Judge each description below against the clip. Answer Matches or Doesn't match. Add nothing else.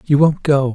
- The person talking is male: Matches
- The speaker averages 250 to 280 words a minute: Doesn't match